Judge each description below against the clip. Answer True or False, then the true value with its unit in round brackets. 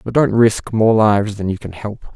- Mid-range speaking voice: False (105 Hz)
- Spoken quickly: True (250 wpm)